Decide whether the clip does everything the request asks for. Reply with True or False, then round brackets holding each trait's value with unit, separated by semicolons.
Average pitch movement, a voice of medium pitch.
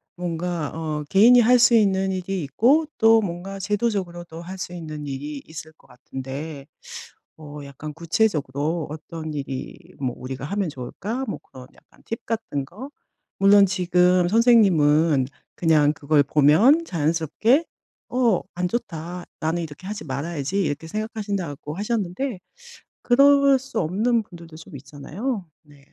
False (5.7 semitones; 175 Hz)